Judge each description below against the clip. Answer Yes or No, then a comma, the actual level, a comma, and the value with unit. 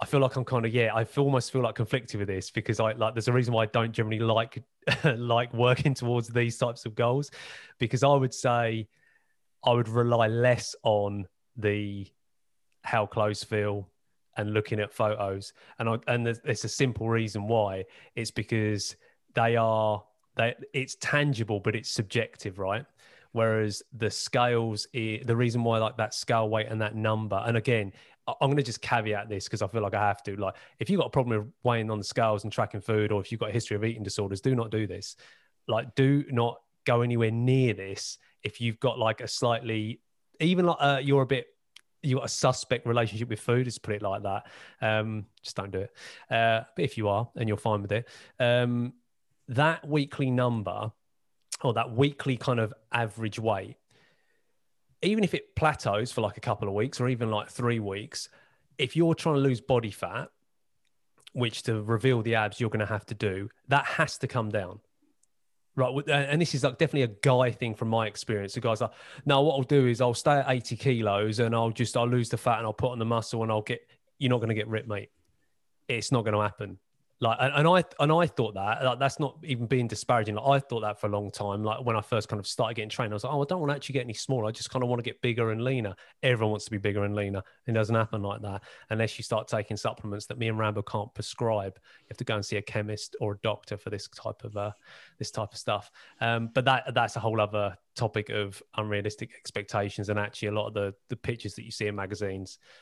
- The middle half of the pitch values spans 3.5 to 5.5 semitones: No, average, 2.9 semitones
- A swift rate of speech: Yes, fast, 230 wpm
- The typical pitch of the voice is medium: No, low, 115 Hz